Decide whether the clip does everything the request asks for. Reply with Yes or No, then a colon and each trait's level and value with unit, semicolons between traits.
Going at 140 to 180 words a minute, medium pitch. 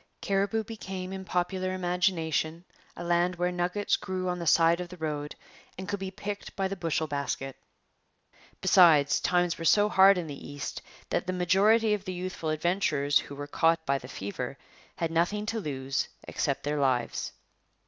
Yes: average, 175 wpm; medium, 175 Hz